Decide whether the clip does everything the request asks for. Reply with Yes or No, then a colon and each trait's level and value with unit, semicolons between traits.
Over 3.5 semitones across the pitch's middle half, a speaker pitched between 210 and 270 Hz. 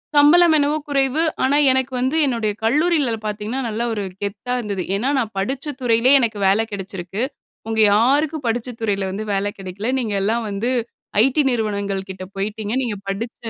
Yes: average, 4.5 semitones; high, 225 Hz